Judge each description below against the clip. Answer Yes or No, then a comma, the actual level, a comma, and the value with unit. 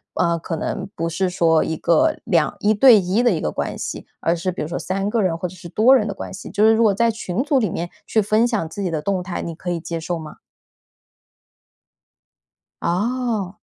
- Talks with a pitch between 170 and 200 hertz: Yes, medium, 185 Hz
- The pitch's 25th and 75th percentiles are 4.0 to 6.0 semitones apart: Yes, average, 4.5 semitones